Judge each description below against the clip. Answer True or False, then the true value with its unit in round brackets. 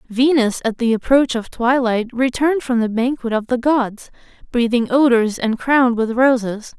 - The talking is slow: False (170 wpm)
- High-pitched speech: True (245 Hz)